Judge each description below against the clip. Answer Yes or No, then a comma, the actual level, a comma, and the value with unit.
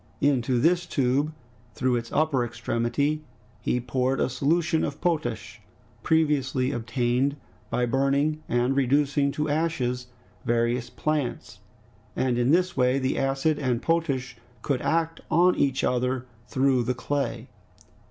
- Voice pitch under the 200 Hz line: Yes, low, 135 Hz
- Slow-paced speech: Yes, slow, 130 wpm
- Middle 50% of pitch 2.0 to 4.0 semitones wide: Yes, average, 3.4 semitones